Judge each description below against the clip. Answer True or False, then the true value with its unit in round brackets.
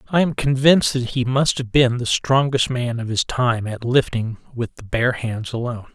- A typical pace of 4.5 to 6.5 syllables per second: True (4.9 syllables/s)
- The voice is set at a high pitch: False (125 Hz)